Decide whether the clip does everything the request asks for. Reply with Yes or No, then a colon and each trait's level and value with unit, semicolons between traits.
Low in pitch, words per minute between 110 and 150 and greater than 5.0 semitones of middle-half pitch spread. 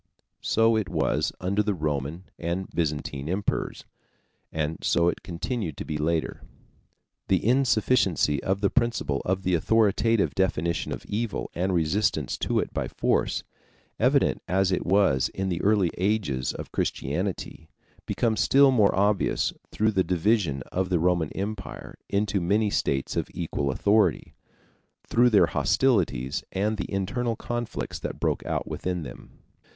No: very low, 95 Hz; average, 145 wpm; average, 4.3 semitones